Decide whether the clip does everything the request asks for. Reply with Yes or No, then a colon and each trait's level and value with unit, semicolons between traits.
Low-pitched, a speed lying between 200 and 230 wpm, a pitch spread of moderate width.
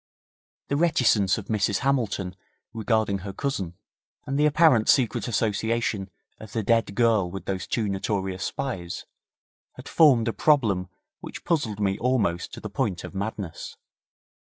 No: low, 110 Hz; average, 145 wpm; average, 4.4 semitones